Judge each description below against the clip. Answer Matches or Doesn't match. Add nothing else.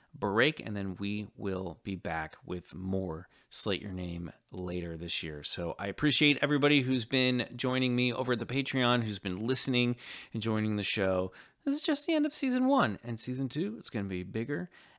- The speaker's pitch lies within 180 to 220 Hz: Doesn't match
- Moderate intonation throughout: Doesn't match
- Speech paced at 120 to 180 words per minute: Doesn't match